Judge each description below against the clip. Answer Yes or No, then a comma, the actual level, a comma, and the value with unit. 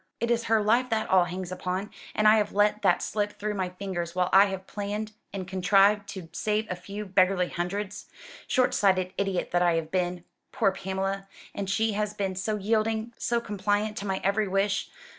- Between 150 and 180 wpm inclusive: No, average, 200 wpm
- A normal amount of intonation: No, narrow, 2.2 semitones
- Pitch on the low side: No, high, 200 Hz